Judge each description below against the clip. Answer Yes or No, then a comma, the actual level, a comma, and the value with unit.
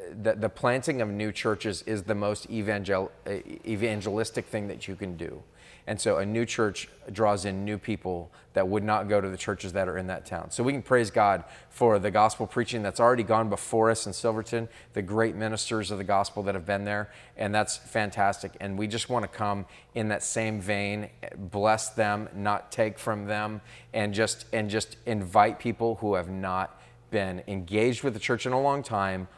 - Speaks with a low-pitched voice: Yes, low, 105 Hz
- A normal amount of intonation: No, narrow, 2.0 semitones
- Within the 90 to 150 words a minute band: No, average, 200 wpm